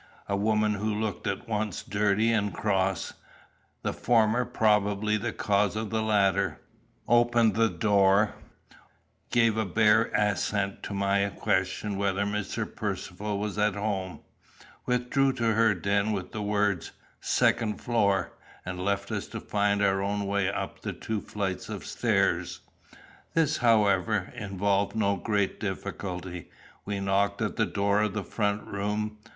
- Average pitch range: No, narrow, 1.5 semitones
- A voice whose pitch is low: Yes, low, 105 Hz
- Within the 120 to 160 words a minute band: Yes, average, 145 wpm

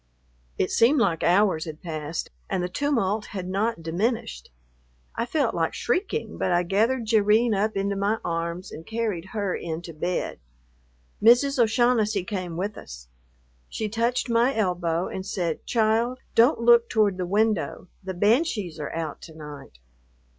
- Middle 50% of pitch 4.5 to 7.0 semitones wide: Yes, average, 4.9 semitones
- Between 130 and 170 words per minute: Yes, average, 155 wpm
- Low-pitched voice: No, high, 200 Hz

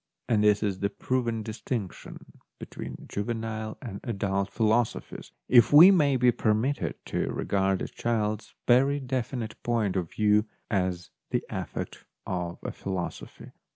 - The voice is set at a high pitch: No, low, 110 Hz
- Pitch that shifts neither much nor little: Yes, average, 3.3 semitones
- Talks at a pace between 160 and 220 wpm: No, average, 145 wpm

